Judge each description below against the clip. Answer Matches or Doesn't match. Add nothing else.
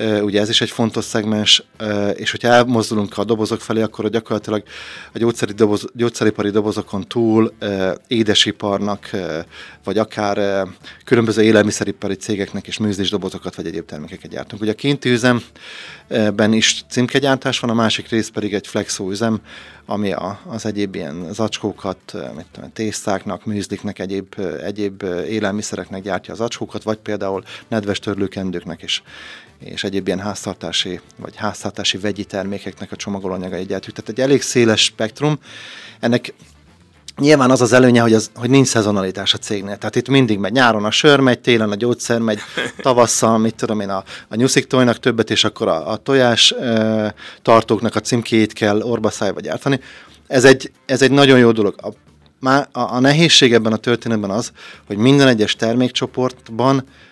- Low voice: Matches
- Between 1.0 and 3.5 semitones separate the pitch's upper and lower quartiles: Matches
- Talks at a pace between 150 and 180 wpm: Matches